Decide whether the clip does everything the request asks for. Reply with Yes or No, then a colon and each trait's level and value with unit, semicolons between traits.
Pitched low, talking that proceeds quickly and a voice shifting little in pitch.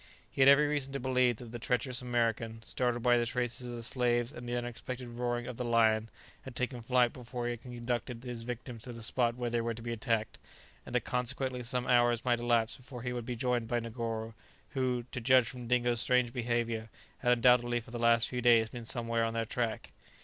Yes: low, 120 Hz; fast, 220 wpm; narrow, 1.1 semitones